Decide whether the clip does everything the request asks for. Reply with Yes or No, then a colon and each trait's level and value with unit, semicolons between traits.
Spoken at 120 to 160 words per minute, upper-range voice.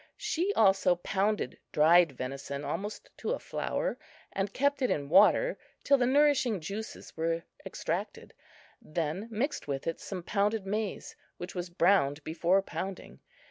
Yes: average, 140 wpm; high, 195 Hz